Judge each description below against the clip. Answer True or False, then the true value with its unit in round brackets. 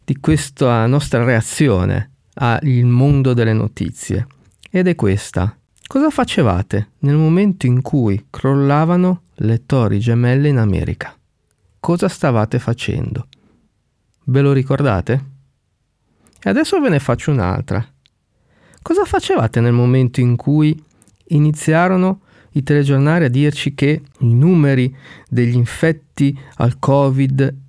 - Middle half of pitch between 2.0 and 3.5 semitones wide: False (4.0 semitones)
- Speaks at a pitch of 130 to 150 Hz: True (135 Hz)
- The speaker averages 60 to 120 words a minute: True (115 wpm)